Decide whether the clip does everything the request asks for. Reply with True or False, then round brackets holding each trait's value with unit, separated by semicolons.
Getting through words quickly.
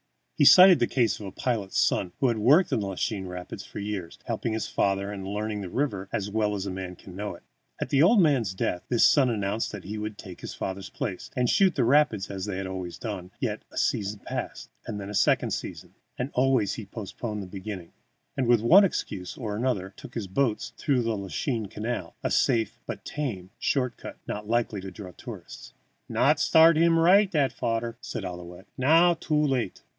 True (210 wpm)